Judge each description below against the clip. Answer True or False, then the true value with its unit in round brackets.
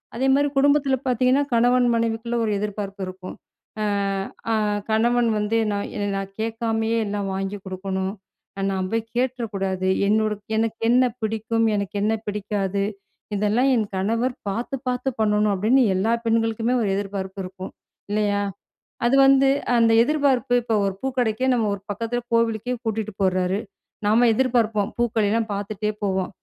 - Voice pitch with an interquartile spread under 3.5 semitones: True (2.9 semitones)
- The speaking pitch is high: True (220 Hz)